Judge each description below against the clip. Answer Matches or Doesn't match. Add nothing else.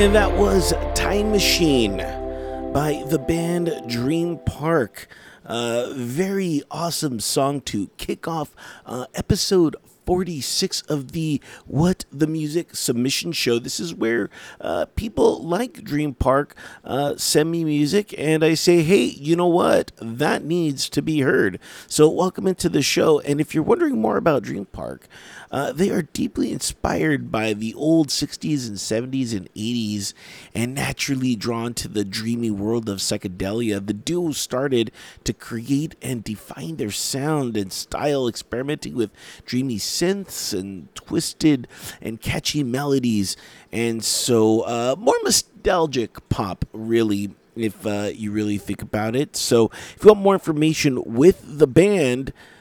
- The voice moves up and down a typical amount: Doesn't match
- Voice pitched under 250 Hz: Matches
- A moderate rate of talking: Matches